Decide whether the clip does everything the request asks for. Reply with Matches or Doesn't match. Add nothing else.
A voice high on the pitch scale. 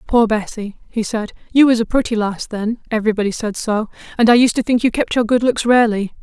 Matches